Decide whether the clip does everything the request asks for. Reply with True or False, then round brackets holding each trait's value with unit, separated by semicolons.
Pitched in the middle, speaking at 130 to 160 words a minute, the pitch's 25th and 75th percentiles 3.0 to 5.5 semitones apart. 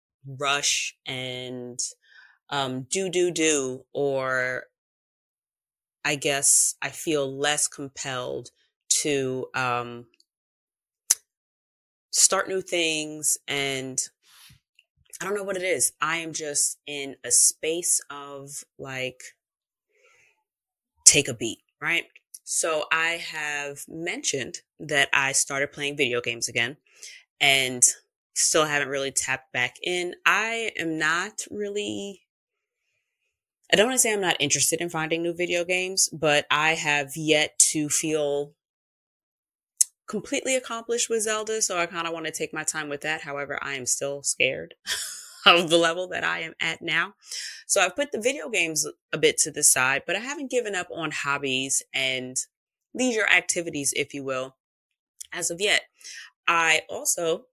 True (155 Hz; 140 wpm; 4.7 semitones)